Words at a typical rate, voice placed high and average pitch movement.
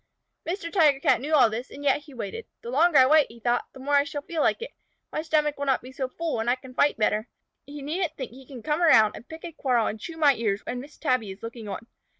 No: fast, 275 wpm; very high, 275 Hz; average, 4.3 semitones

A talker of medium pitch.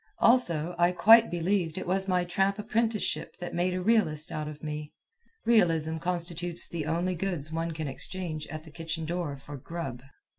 Yes: medium, 170 Hz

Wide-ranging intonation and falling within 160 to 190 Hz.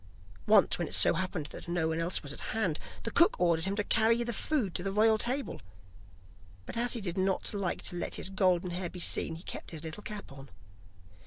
No: average, 4.2 semitones; medium, 185 Hz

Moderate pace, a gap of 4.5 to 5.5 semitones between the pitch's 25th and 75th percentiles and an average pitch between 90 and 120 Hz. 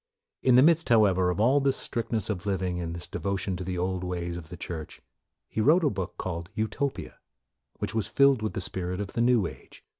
No: fast, 230 wpm; average, 4.8 semitones; very low, 95 Hz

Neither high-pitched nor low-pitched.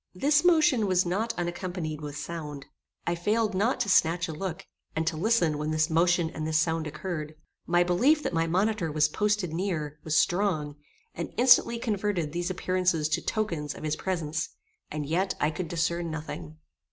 Yes: medium, 170 Hz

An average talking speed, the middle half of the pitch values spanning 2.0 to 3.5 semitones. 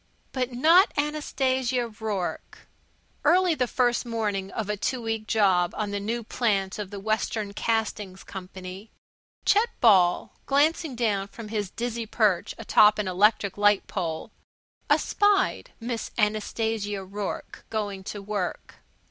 No: slow, 130 wpm; average, 3.2 semitones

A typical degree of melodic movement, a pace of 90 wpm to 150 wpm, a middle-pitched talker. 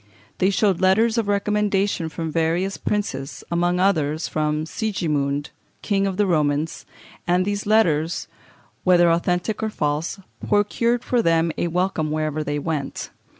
Yes: average, 4.5 semitones; average, 140 wpm; medium, 175 Hz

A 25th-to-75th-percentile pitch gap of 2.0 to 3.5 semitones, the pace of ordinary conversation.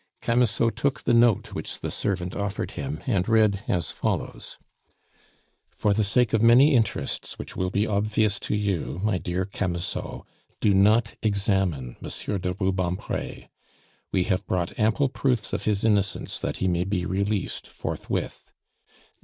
Yes: average, 3.1 semitones; average, 150 wpm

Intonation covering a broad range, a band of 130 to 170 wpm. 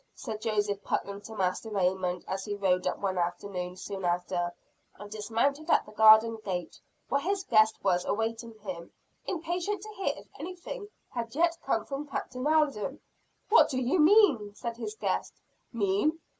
Yes: wide, 7.2 semitones; average, 165 wpm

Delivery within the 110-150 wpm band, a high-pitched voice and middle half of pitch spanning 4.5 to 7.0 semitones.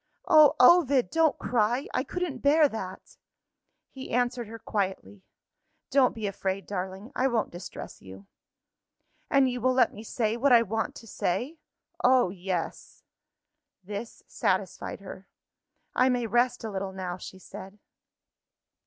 Yes: average, 140 wpm; high, 230 Hz; average, 5.0 semitones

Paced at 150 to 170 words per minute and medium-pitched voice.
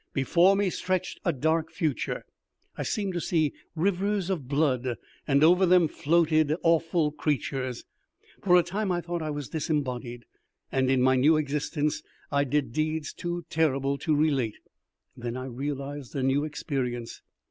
Yes: average, 155 wpm; medium, 150 Hz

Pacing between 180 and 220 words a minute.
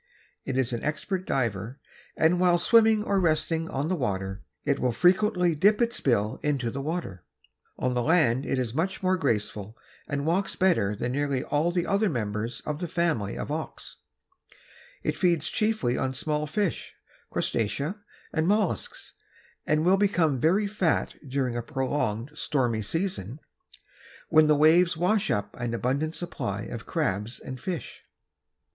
No: average, 155 wpm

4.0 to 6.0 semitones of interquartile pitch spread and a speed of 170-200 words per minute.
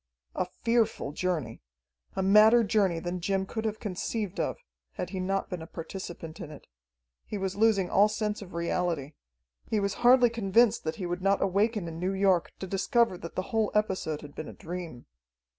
No: average, 3.6 semitones; average, 190 wpm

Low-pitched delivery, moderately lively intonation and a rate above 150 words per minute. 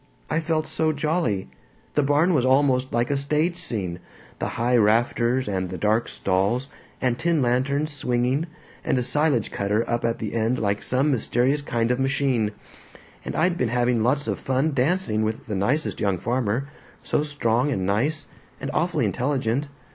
Yes: low, 125 Hz; average, 4.3 semitones; average, 170 wpm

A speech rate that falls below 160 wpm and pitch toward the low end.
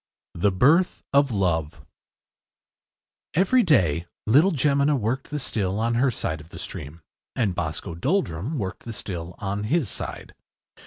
Yes: average, 145 wpm; low, 110 Hz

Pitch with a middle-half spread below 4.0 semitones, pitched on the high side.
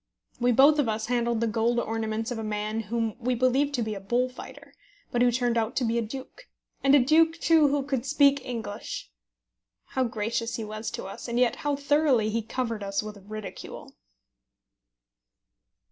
Yes: average, 3.3 semitones; high, 235 Hz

